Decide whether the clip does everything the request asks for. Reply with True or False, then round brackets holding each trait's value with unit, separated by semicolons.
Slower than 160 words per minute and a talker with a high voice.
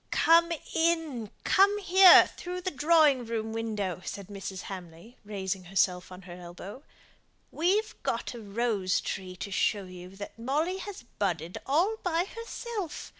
True (145 wpm; 225 Hz)